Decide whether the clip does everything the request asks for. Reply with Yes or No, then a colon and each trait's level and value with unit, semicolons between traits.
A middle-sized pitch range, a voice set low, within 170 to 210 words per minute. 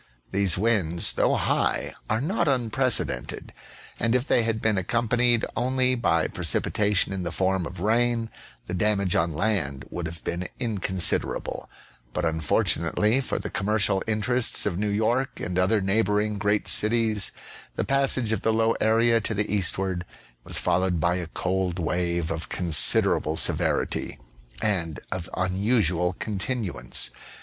No: average, 4.3 semitones; low, 100 Hz; average, 145 wpm